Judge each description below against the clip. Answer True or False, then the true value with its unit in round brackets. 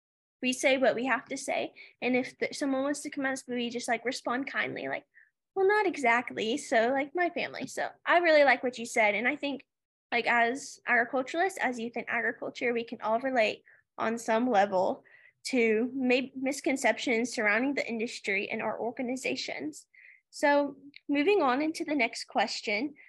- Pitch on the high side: True (255 Hz)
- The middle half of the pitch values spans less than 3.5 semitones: False (3.9 semitones)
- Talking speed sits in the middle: True (175 wpm)